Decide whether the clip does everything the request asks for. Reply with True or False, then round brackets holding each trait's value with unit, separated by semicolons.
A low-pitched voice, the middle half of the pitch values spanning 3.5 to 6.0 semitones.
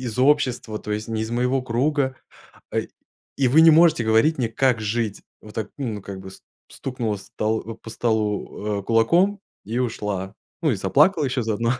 True (115 Hz; 3.8 semitones)